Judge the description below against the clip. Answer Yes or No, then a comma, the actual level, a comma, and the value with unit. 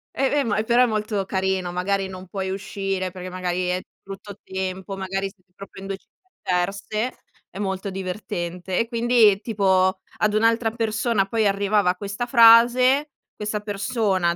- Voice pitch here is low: No, high, 195 Hz